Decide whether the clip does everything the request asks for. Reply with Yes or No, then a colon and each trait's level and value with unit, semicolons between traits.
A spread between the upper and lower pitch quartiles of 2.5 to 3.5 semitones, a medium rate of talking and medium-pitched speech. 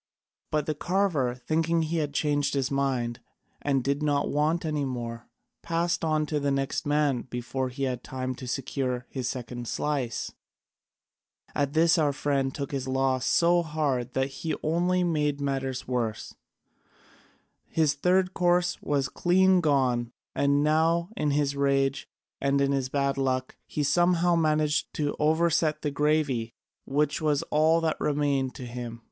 Yes: average, 2.9 semitones; average, 150 wpm; medium, 145 Hz